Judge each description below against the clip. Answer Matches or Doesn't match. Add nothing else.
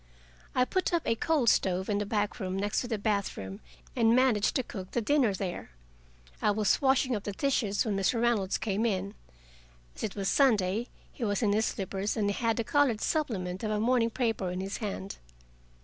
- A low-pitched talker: Doesn't match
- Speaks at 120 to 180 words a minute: Doesn't match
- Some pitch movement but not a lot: Matches